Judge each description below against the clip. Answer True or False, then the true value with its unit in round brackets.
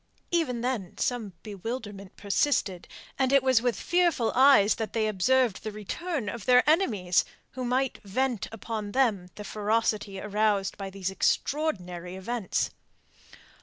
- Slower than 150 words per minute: True (135 wpm)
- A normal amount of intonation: True (4.6 semitones)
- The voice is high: True (220 Hz)